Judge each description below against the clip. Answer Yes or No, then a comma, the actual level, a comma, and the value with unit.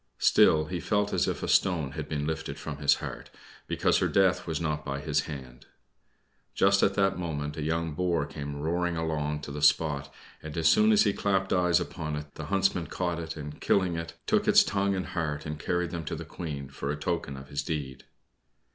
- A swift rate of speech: Yes, fast, 215 wpm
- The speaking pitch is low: Yes, very low, 80 Hz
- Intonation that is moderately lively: Yes, average, 3.3 semitones